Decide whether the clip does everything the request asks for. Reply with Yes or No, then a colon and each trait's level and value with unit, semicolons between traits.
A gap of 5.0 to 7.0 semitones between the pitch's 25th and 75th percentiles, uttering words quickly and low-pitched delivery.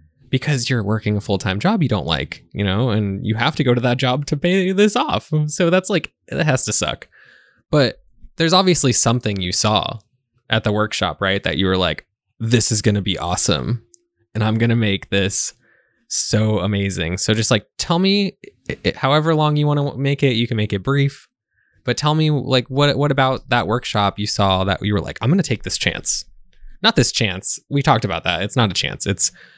Yes: wide, 5.5 semitones; fast, 220 wpm; low, 115 Hz